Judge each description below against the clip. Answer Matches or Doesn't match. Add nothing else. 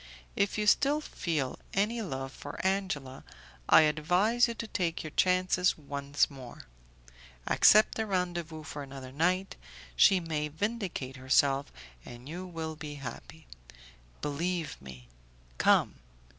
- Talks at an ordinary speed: Doesn't match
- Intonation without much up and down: Doesn't match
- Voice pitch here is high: Doesn't match